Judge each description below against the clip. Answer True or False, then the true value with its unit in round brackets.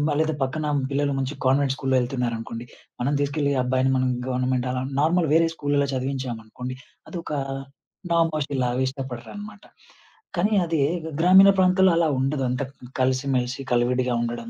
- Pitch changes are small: False (3.7 semitones)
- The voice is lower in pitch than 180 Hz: True (135 Hz)